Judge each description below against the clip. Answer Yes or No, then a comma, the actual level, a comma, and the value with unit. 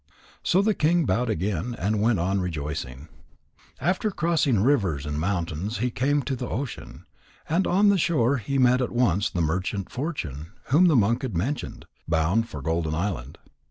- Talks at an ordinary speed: Yes, average, 170 wpm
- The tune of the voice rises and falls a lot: Yes, wide, 8.6 semitones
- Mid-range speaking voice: No, low, 110 Hz